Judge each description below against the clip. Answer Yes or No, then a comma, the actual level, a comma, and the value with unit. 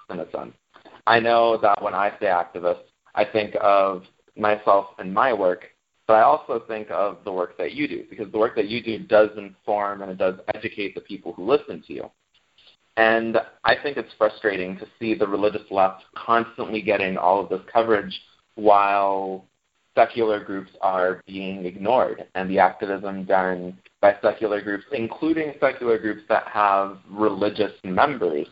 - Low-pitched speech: Yes, low, 105 Hz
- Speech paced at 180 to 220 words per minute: No, average, 165 wpm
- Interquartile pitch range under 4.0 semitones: Yes, average, 2.7 semitones